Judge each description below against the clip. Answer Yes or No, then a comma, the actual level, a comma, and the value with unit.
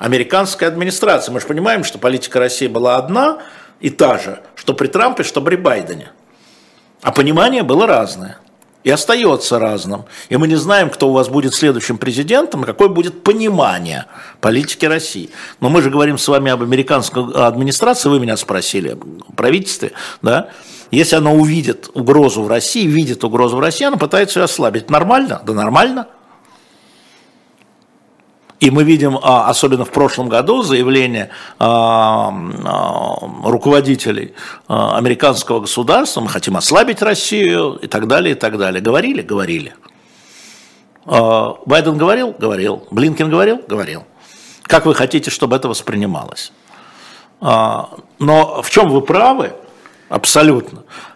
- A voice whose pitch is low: No, medium, 145 Hz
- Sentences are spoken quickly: No, average, 135 wpm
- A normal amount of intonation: No, wide, 6.1 semitones